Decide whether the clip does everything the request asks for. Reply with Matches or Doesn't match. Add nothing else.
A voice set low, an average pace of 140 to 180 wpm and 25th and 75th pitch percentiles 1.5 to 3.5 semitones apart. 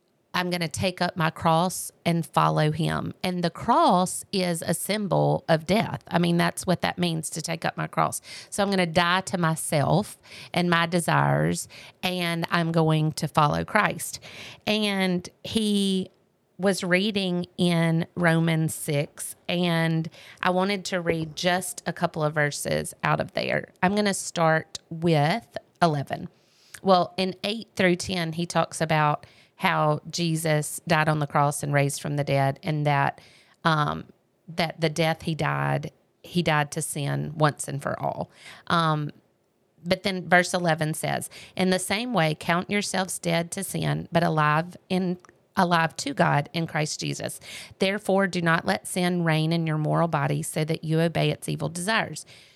Doesn't match